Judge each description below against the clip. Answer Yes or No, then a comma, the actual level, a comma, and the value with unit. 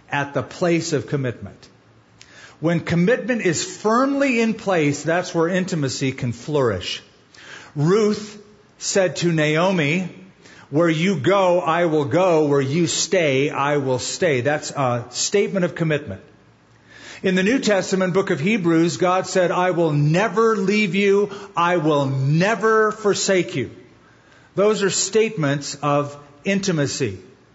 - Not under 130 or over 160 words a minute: Yes, slow, 135 wpm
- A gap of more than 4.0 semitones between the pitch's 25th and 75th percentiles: Yes, average, 5.2 semitones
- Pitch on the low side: No, medium, 175 Hz